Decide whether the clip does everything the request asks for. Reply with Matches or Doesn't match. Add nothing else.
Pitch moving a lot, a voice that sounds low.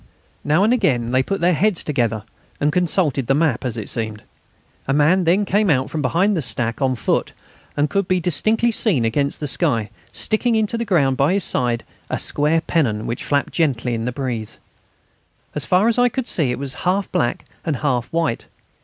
Doesn't match